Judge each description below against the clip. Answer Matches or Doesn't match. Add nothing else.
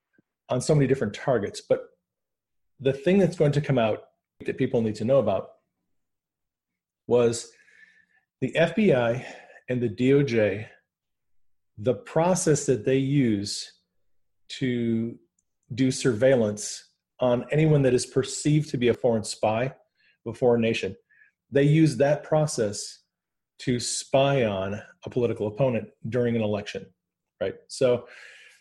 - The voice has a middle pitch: Doesn't match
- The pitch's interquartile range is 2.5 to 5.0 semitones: Matches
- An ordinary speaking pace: Doesn't match